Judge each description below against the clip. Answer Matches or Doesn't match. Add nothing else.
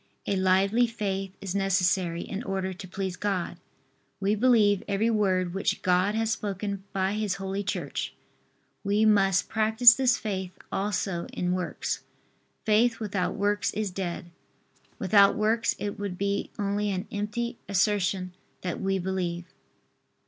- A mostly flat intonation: Matches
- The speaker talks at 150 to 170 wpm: Doesn't match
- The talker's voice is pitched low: Doesn't match